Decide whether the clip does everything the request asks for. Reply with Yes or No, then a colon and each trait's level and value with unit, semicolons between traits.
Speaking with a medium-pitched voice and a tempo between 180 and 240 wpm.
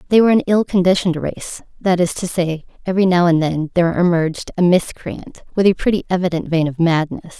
Yes: medium, 175 Hz; average, 195 wpm